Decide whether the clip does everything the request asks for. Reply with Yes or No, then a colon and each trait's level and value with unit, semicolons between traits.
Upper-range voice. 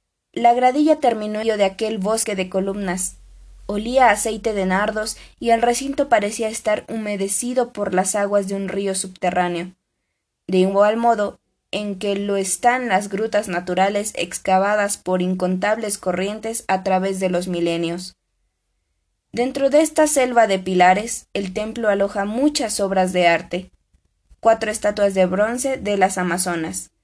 Yes: high, 205 Hz